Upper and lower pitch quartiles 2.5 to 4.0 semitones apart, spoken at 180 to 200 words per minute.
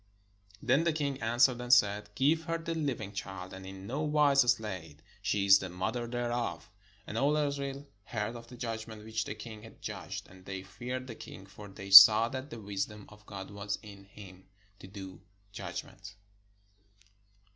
No: average, 4.5 semitones; average, 185 wpm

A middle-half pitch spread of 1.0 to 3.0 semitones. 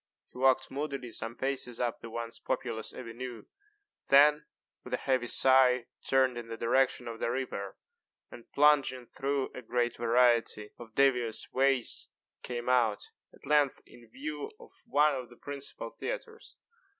Yes: narrow, 2.6 semitones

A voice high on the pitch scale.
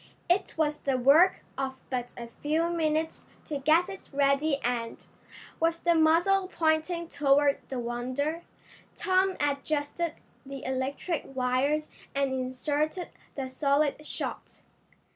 Yes: very high, 290 Hz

